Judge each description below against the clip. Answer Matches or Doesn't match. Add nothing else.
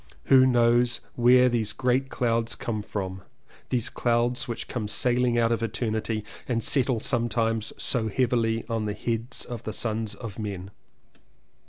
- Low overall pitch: Matches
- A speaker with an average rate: Matches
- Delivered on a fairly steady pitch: Matches